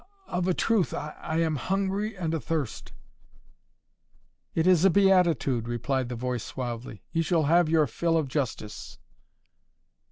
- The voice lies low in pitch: No, medium, 160 Hz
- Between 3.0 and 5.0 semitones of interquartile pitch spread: No, wide, 5.6 semitones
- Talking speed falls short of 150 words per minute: Yes, average, 140 wpm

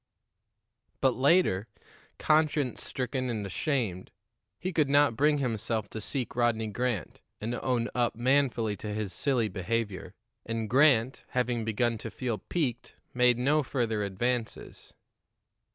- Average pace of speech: No, slow, 130 wpm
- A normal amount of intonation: Yes, average, 3.3 semitones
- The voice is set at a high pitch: No, low, 120 Hz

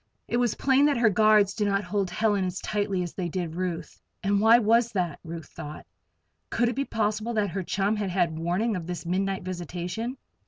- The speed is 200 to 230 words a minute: Yes, fast, 205 wpm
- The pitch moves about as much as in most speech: Yes, average, 3.7 semitones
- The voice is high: Yes, high, 195 Hz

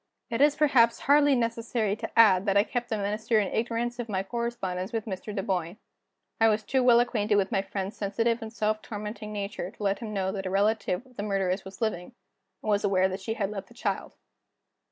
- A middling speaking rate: No, fast, 215 wpm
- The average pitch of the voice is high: Yes, high, 215 Hz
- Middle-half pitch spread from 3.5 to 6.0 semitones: No, average, 2.9 semitones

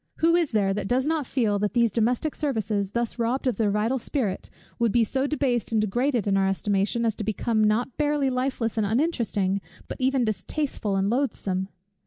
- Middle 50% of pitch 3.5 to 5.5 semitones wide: Yes, average, 4.3 semitones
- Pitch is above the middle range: Yes, high, 230 Hz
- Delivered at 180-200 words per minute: Yes, average, 195 wpm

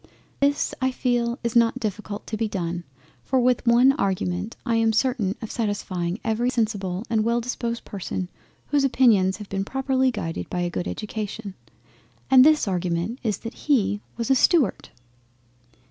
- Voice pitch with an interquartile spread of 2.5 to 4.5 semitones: Yes, average, 4.2 semitones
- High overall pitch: Yes, high, 225 Hz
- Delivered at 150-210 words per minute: Yes, average, 160 wpm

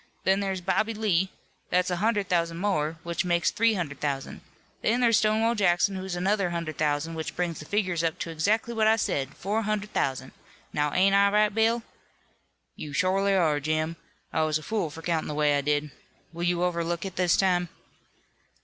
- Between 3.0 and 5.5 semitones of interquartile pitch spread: Yes, average, 4.3 semitones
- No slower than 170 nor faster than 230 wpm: Yes, average, 195 wpm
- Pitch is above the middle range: No, medium, 180 Hz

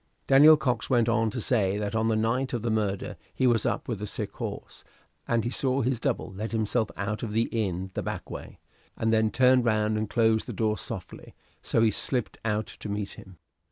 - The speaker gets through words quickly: Yes, fast, 220 wpm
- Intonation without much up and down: Yes, narrow, 2.1 semitones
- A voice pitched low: Yes, low, 110 Hz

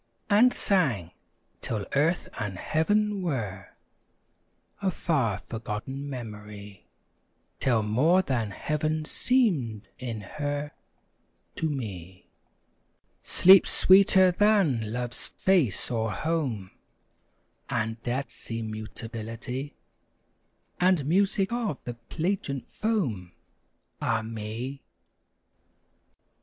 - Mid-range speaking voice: No, low, 130 Hz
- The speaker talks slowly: Yes, slow, 85 wpm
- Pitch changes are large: Yes, wide, 7.8 semitones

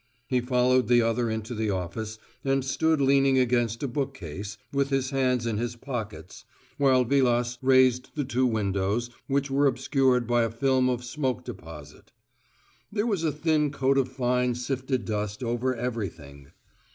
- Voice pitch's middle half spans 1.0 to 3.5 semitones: Yes, average, 2.8 semitones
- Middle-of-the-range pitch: No, low, 125 Hz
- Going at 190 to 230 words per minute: No, average, 160 wpm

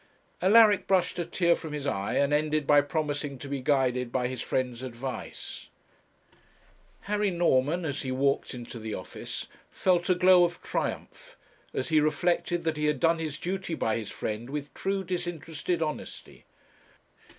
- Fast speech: No, average, 160 wpm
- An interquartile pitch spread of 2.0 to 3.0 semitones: No, average, 4.9 semitones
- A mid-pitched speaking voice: Yes, medium, 150 Hz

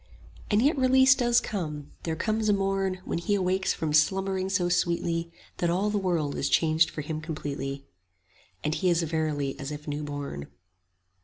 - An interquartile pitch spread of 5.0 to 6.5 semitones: No, average, 4.3 semitones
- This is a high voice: No, medium, 170 Hz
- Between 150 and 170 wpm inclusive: No, average, 180 wpm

